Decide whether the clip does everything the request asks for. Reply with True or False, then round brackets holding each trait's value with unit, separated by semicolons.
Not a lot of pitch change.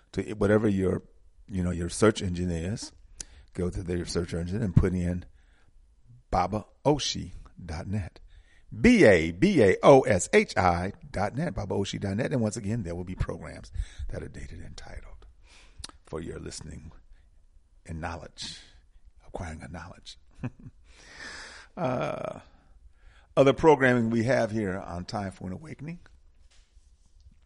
False (5.1 semitones)